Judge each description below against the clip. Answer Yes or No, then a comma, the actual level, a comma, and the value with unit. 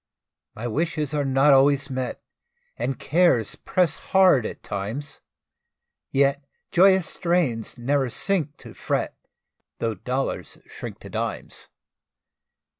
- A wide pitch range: No, average, 4.5 semitones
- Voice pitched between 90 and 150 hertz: Yes, medium, 140 Hz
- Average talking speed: No, slow, 115 wpm